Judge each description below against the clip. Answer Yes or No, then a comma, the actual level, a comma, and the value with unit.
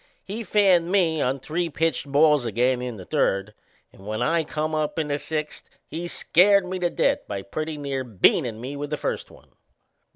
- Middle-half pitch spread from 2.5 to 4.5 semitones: No, average, 5.0 semitones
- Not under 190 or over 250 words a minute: Yes, average, 195 wpm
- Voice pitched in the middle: Yes, medium, 150 Hz